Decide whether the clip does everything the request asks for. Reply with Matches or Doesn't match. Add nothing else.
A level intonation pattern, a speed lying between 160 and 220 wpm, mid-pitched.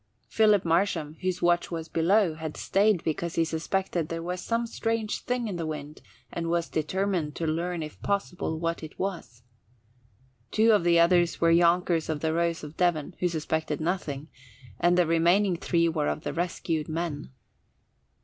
Matches